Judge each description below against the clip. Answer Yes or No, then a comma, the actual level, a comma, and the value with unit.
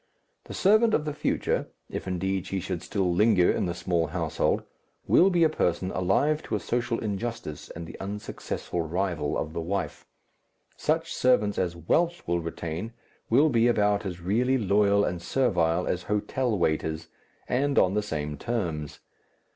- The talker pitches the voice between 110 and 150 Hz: No, low, 100 Hz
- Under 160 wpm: No, average, 165 wpm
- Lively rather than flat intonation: Yes, wide, 5.8 semitones